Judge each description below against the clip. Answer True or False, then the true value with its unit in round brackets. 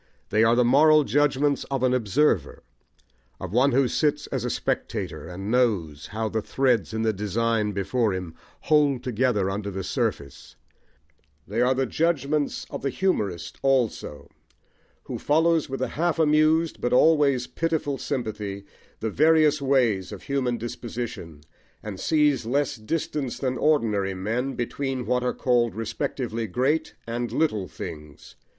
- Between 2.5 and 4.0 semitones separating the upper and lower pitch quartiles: False (5.1 semitones)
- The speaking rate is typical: True (145 wpm)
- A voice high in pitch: False (125 Hz)